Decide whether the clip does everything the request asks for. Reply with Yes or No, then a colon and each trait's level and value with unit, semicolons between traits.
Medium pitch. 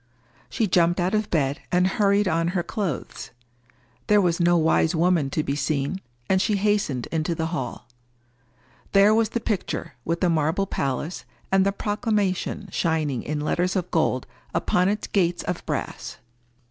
Yes: medium, 175 Hz